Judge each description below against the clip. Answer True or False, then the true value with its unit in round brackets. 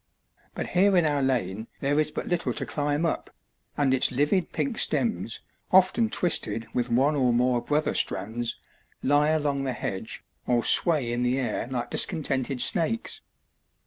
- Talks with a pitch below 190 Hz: True (140 Hz)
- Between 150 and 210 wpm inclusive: True (160 wpm)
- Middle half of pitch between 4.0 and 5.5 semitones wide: True (4.6 semitones)